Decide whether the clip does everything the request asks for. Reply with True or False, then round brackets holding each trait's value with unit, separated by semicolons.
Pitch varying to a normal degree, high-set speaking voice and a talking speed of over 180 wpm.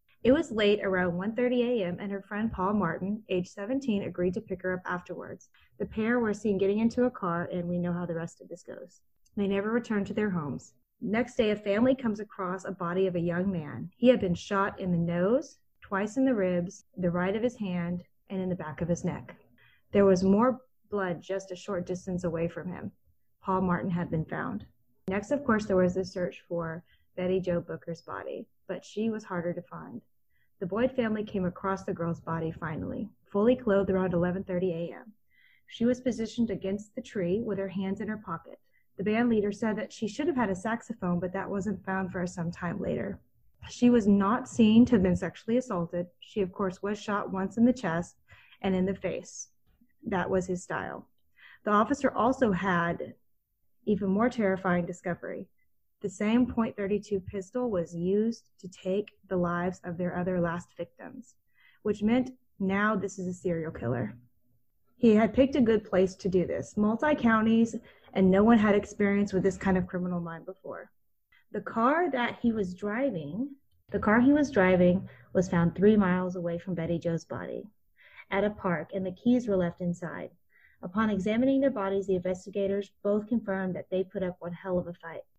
True (3.5 semitones; 195 Hz; 200 wpm)